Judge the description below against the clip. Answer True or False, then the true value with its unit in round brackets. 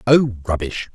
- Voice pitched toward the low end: True (105 Hz)